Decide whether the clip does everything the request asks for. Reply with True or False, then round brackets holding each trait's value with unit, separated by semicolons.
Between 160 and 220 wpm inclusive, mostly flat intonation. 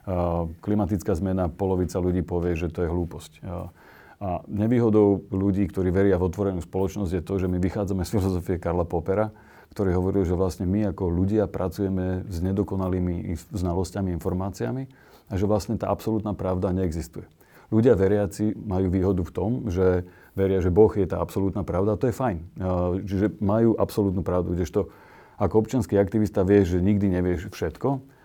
True (165 wpm; 2.3 semitones)